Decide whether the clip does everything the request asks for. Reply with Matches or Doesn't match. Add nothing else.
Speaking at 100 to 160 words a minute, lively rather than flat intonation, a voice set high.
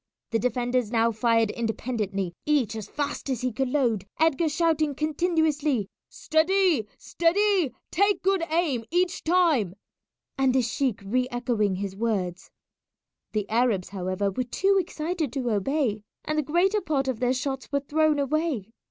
Matches